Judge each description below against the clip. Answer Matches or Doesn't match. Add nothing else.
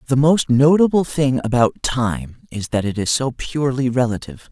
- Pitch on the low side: Matches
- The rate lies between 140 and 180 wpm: Matches